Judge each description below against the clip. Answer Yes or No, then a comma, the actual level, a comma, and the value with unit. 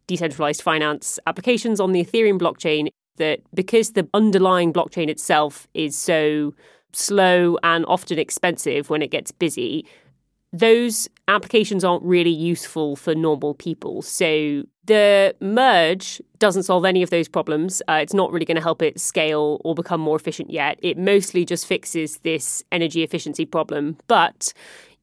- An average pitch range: Yes, average, 3.5 semitones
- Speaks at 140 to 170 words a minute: Yes, average, 150 wpm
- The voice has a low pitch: No, medium, 170 Hz